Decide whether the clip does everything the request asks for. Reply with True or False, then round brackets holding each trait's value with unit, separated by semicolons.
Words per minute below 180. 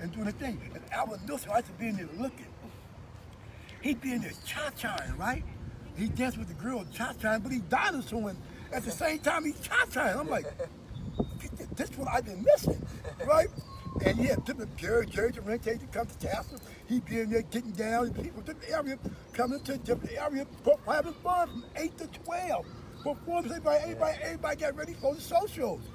False (205 wpm)